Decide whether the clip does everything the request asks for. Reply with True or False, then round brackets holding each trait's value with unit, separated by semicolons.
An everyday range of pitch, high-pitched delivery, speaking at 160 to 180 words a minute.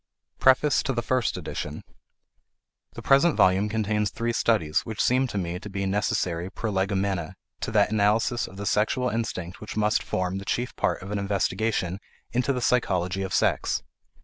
False (3.5 semitones; 105 Hz; 170 wpm)